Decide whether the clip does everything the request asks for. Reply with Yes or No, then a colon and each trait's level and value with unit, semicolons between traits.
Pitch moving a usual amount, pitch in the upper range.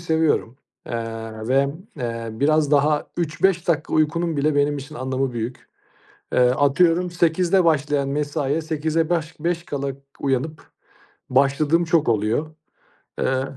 No: average, 3.1 semitones; medium, 150 Hz